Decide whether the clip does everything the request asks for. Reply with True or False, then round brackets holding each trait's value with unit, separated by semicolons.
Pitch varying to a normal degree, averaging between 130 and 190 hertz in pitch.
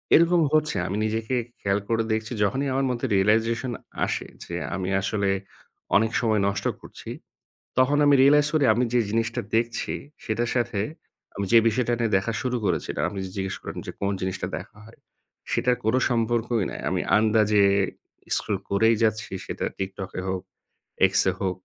False (3.4 semitones; 110 Hz)